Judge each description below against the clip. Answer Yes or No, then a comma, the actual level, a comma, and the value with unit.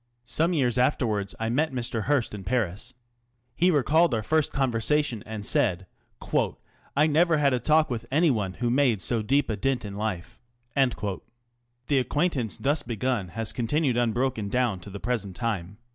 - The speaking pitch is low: Yes, low, 120 Hz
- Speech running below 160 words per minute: No, average, 170 wpm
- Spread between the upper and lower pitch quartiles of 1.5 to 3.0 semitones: No, average, 4.5 semitones